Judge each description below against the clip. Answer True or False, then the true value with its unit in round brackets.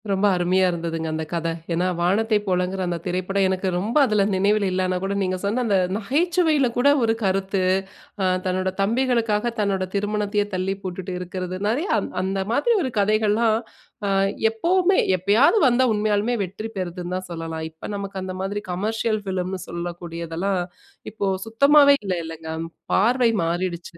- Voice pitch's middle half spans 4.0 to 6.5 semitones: False (3.4 semitones)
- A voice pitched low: False (195 Hz)